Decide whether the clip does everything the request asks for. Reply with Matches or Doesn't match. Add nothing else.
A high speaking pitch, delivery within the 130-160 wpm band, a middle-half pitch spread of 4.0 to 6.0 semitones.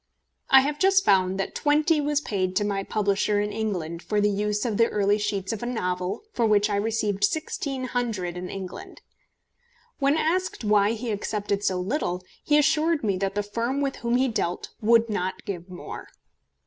Doesn't match